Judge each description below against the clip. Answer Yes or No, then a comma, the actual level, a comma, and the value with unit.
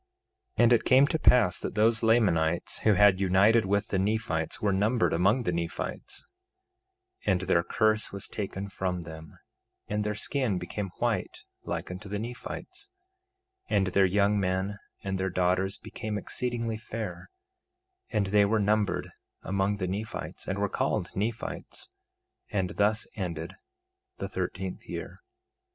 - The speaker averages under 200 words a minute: Yes, average, 150 wpm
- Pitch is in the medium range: No, low, 100 Hz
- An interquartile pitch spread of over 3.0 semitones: No, average, 2.7 semitones